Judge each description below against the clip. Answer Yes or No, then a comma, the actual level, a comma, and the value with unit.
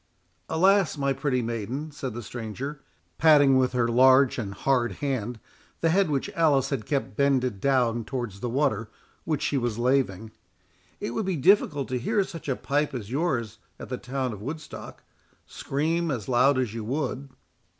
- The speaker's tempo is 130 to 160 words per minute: No, average, 170 wpm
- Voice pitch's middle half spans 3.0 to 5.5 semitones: Yes, average, 3.6 semitones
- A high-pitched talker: No, low, 130 Hz